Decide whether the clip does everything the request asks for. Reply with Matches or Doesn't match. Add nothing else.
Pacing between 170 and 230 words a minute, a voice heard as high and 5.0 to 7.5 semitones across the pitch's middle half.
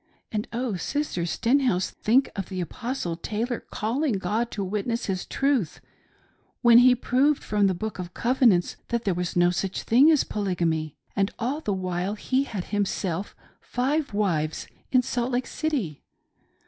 Doesn't match